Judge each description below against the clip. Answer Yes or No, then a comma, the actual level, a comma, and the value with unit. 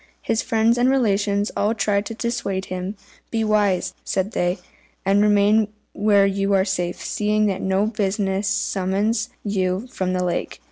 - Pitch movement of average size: No, narrow, 2.0 semitones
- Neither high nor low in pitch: No, high, 200 Hz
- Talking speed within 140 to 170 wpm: Yes, average, 155 wpm